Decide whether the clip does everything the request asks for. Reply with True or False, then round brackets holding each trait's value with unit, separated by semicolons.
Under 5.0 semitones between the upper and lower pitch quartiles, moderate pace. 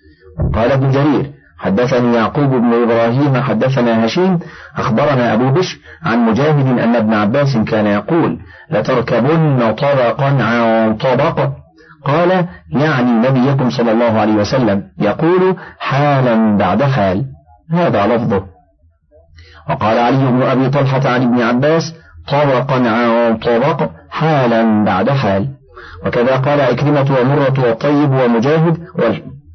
True (4.2 semitones; 115 wpm)